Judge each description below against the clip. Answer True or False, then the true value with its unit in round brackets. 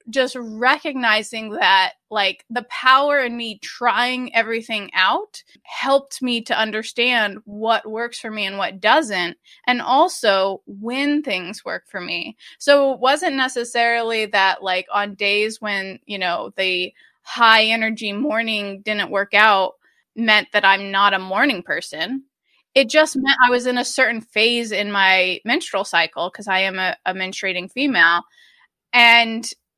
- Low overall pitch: False (225 Hz)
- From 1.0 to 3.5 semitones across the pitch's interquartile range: False (4.2 semitones)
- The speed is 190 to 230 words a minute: False (150 wpm)